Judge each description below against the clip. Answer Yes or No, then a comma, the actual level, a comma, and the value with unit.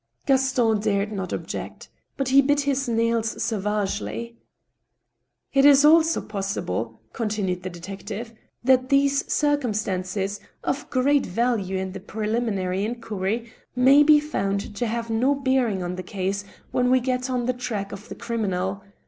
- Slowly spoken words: No, average, 155 wpm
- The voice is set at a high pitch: Yes, high, 225 Hz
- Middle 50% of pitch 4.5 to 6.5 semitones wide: Yes, average, 5.0 semitones